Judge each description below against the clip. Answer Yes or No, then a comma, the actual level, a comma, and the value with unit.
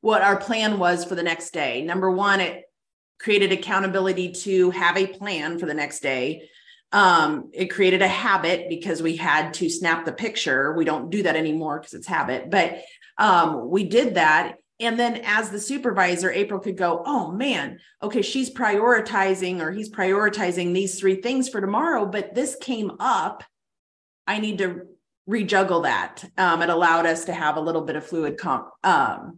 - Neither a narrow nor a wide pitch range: Yes, average, 3.6 semitones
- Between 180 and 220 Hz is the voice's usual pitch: Yes, high, 190 Hz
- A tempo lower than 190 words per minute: Yes, average, 180 wpm